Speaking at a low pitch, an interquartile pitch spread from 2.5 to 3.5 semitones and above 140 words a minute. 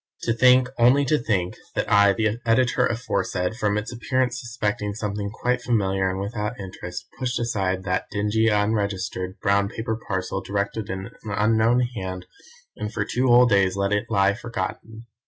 Yes: low, 105 Hz; average, 3.2 semitones; average, 165 wpm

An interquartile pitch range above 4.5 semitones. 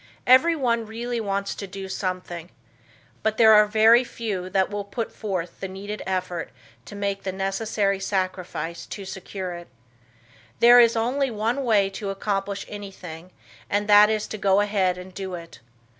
No: narrow, 2.6 semitones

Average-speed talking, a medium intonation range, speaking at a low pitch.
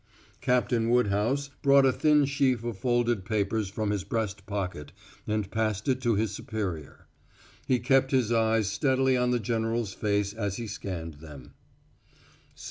Yes: average, 150 wpm; average, 3.5 semitones; low, 110 Hz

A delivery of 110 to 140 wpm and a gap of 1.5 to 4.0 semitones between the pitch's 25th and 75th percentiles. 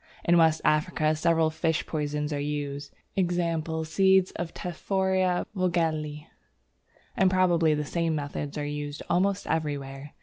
Yes: slow, 135 wpm; average, 2.9 semitones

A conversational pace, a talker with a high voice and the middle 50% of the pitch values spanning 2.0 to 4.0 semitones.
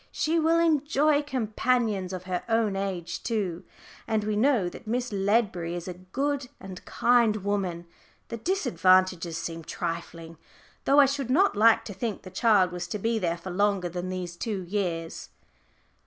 No: average, 165 wpm; high, 200 Hz; average, 5.1 semitones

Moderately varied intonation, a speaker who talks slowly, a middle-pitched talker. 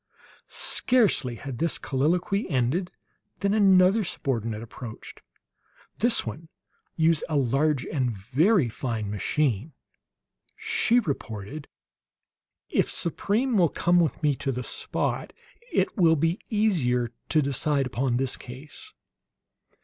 No: wide, 6.6 semitones; slow, 115 wpm; medium, 150 Hz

